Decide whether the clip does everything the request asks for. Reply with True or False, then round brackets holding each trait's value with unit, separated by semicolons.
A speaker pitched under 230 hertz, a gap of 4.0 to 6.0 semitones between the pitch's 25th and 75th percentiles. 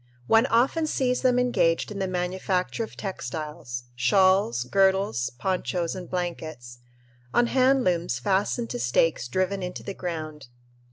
True (185 Hz; 4.7 semitones)